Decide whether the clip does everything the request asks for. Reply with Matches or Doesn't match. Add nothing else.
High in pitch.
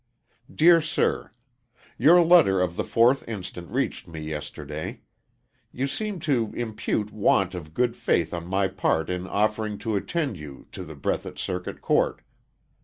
Doesn't match